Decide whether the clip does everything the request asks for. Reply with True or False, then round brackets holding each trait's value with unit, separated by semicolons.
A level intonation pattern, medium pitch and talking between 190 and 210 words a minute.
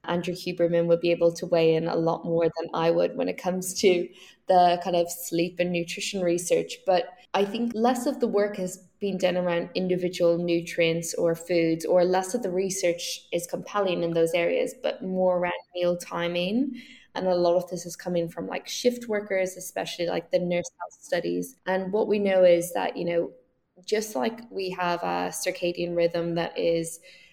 True (1.7 semitones; 175 Hz; 195 wpm)